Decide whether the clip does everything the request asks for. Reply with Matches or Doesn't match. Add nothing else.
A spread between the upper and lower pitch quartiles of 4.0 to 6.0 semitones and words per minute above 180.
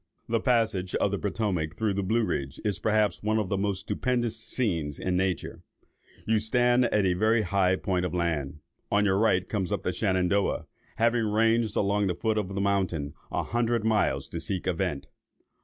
Doesn't match